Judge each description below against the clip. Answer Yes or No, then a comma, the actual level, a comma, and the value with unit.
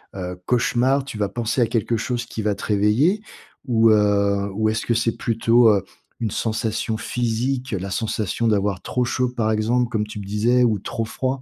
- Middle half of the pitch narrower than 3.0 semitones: Yes, narrow, 2.6 semitones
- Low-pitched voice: Yes, low, 115 Hz